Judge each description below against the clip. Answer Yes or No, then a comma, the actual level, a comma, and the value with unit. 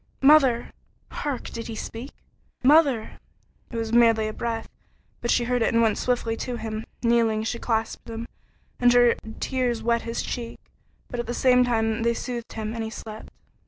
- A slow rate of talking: No, average, 175 wpm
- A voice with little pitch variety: Yes, narrow, 1.5 semitones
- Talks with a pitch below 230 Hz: No, high, 235 Hz